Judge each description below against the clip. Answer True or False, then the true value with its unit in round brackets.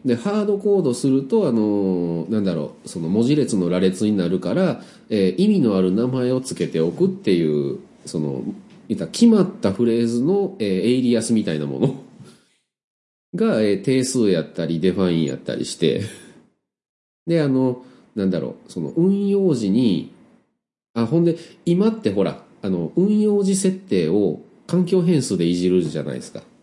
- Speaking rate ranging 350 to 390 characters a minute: False (315 characters per minute)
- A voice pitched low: True (125 Hz)